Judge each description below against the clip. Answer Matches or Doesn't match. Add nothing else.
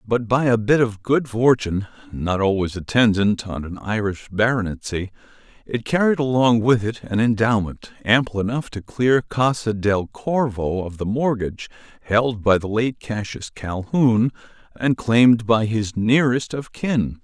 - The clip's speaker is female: Doesn't match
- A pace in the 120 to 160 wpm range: Matches